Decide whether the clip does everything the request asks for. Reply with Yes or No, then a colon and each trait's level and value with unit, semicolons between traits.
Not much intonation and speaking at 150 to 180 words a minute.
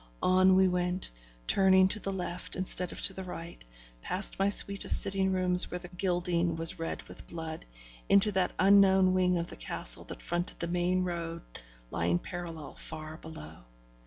Yes: narrow, 1.9 semitones; average, 175 wpm